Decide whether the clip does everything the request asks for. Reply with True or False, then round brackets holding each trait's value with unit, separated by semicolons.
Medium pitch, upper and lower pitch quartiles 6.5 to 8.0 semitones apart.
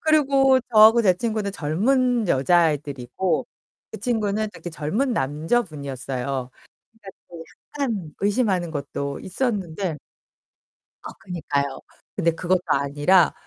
True (180 Hz; 7.1 semitones)